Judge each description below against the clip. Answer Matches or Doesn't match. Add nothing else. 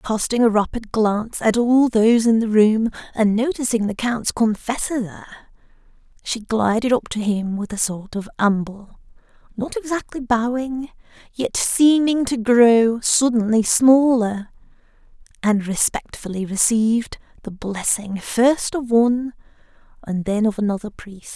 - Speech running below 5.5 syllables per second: Matches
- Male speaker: Doesn't match